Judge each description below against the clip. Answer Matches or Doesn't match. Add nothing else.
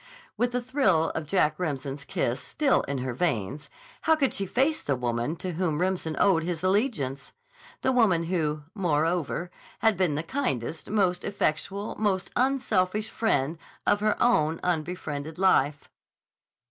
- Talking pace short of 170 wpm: Matches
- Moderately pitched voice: Matches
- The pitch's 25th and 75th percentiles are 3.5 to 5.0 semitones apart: Doesn't match